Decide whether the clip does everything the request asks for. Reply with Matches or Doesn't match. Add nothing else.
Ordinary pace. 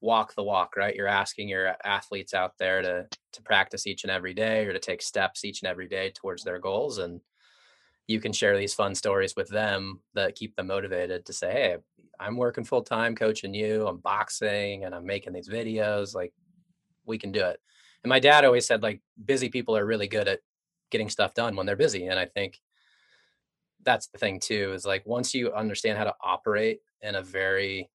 Doesn't match